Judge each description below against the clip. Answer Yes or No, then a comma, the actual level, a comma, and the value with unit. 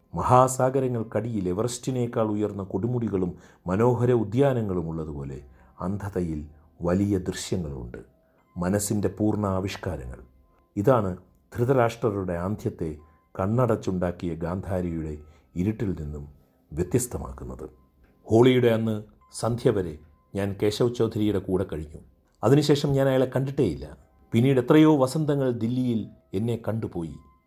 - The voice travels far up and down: Yes, wide, 6.4 semitones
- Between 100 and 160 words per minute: No, average, 85 wpm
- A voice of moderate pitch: No, very low, 95 Hz